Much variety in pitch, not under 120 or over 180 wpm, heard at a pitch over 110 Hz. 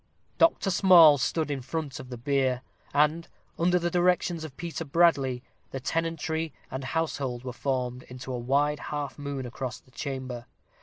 No: average, 4.1 semitones; average, 160 wpm; medium, 140 Hz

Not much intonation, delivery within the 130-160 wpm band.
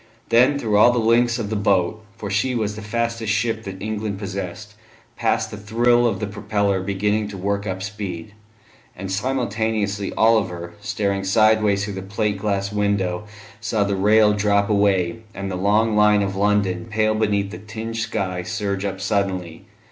No: narrow, 1.9 semitones; average, 170 wpm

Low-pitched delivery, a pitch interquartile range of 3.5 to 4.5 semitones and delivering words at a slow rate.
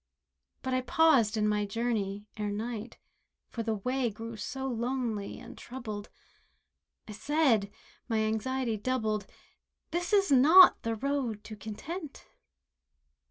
No: high, 230 Hz; average, 3.8 semitones; slow, 120 wpm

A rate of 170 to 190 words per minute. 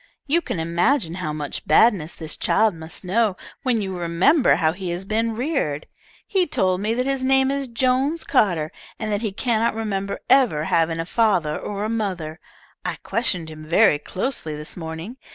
Yes: average, 180 wpm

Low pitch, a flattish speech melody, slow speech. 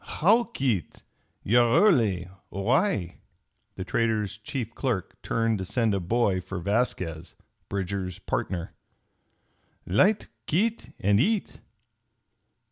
No: low, 110 Hz; wide, 5.5 semitones; slow, 105 wpm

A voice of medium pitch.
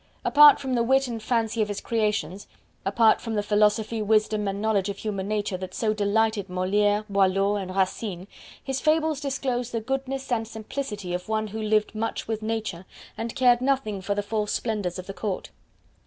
No: high, 215 Hz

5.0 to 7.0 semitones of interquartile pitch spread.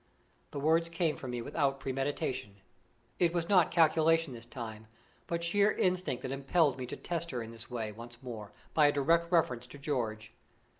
Yes: wide, 5.6 semitones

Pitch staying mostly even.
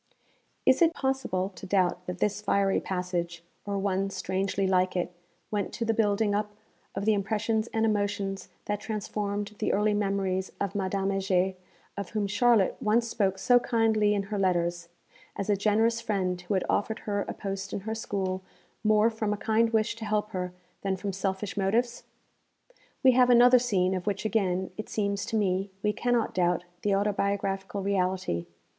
Yes: narrow, 2.2 semitones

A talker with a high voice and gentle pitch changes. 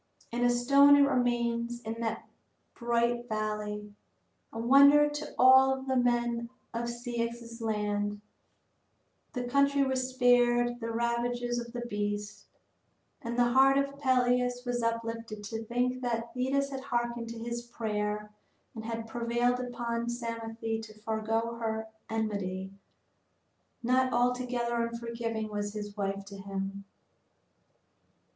Yes: high, 235 Hz; narrow, 1.7 semitones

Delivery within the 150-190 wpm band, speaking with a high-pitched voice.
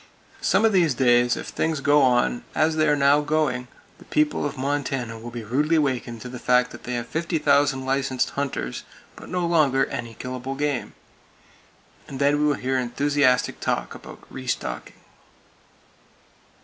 No: average, 160 wpm; low, 135 Hz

